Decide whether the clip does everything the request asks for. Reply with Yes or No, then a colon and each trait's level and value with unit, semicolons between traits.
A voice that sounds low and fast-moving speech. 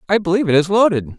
No: medium, 180 Hz; fast, 255 wpm